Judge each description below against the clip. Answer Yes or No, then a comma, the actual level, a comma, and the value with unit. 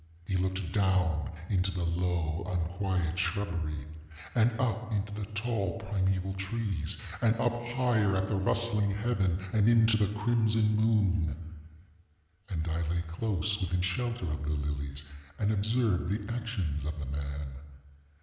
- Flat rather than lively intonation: No, average, 4.4 semitones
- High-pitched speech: No, very low, 95 Hz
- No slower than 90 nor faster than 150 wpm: Yes, average, 140 wpm